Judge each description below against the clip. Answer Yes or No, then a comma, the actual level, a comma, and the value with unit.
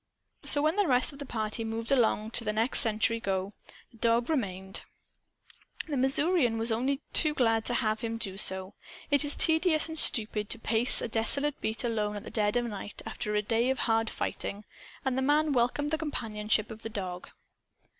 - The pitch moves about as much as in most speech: Yes, average, 4.2 semitones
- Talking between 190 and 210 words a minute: Yes, average, 195 wpm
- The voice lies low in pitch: No, high, 230 Hz